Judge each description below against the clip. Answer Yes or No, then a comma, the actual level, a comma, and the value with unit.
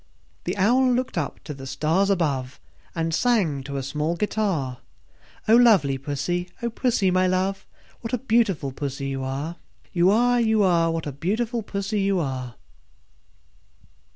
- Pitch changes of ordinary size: No, wide, 7.3 semitones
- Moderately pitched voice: Yes, medium, 180 Hz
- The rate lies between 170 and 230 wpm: No, average, 155 wpm